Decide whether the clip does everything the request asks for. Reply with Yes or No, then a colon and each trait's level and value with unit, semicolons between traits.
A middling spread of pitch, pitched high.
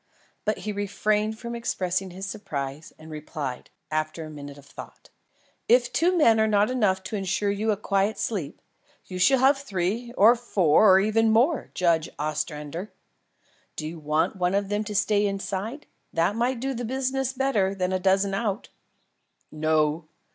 Yes: average, 5.0 semitones; high, 200 Hz